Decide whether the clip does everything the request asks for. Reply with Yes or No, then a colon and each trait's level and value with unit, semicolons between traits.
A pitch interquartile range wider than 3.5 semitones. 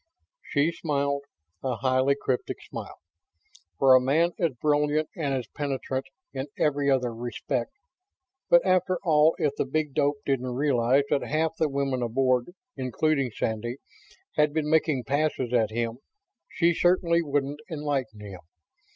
No: average, 3.2 semitones